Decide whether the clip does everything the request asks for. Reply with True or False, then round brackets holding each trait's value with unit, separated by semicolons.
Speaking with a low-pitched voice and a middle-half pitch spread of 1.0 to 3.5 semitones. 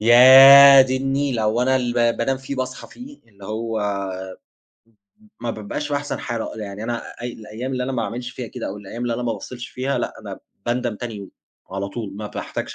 True (120 Hz; 3.0 semitones)